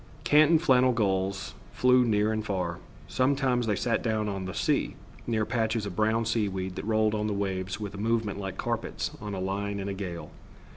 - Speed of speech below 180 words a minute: No, average, 195 wpm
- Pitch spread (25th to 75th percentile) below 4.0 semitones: Yes, average, 2.9 semitones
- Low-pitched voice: Yes, low, 105 Hz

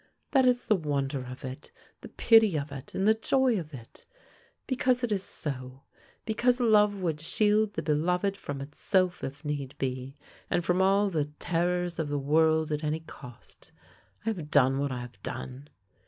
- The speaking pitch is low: No, medium, 160 Hz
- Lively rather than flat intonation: Yes, wide, 6.4 semitones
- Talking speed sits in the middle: Yes, average, 180 wpm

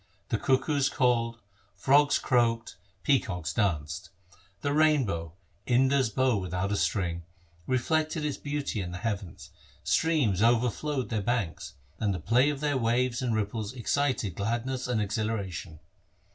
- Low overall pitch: Yes, low, 115 Hz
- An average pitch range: Yes, average, 5.0 semitones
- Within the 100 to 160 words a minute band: Yes, average, 145 wpm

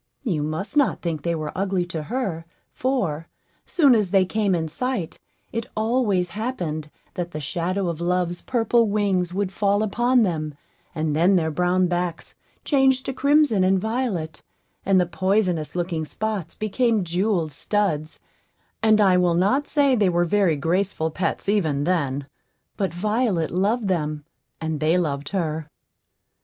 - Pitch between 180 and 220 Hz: Yes, medium, 185 Hz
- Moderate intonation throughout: Yes, average, 4.6 semitones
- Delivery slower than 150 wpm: No, average, 155 wpm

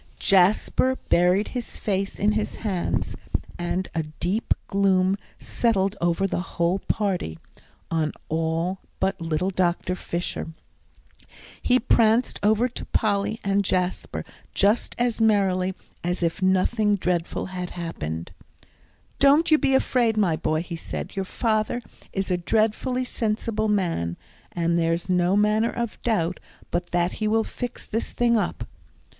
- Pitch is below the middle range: No, high, 195 Hz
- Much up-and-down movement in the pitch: No, average, 3.8 semitones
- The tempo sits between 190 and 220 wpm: No, average, 140 wpm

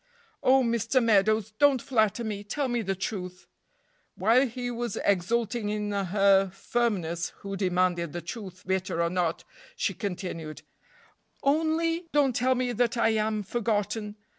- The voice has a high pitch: Yes, high, 210 Hz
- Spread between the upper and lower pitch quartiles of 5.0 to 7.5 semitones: No, average, 4.1 semitones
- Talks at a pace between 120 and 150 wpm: Yes, average, 140 wpm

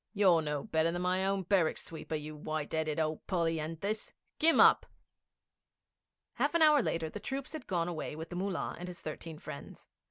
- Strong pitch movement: No, average, 3.8 semitones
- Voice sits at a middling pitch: Yes, medium, 165 Hz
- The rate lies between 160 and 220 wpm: Yes, average, 185 wpm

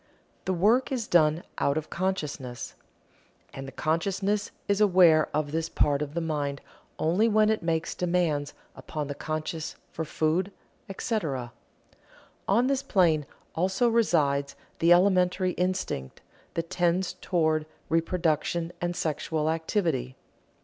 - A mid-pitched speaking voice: Yes, medium, 165 Hz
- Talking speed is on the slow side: Yes, slow, 130 wpm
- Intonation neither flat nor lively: Yes, average, 3.5 semitones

